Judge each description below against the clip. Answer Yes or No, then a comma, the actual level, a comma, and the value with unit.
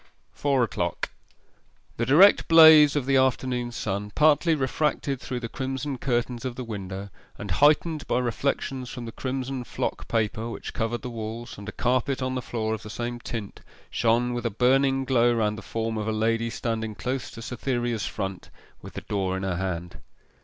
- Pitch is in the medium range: No, low, 120 Hz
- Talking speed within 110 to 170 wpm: No, average, 185 wpm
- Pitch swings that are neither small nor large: Yes, average, 3.1 semitones